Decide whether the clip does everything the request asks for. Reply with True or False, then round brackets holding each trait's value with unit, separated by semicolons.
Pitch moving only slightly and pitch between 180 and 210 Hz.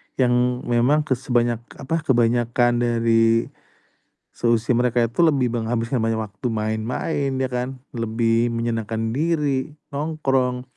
False (2.3 semitones; 120 Hz)